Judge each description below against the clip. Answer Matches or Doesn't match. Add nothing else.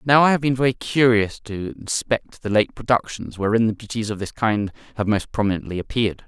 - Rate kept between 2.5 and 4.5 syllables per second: Doesn't match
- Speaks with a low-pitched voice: Matches